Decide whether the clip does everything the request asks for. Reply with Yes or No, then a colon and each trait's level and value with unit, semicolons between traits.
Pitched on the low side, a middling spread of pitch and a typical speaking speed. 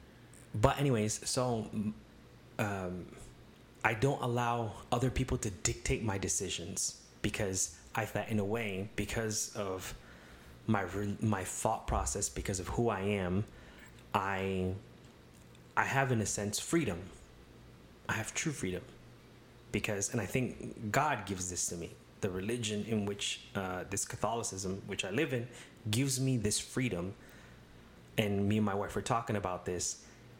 Yes: low, 105 Hz; average, 3.7 semitones; average, 145 wpm